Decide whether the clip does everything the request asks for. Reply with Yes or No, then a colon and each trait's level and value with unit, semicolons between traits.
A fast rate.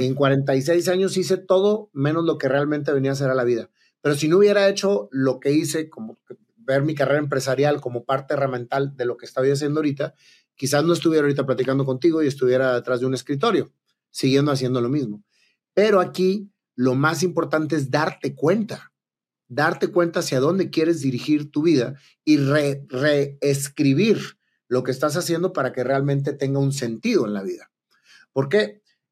No: average, 180 wpm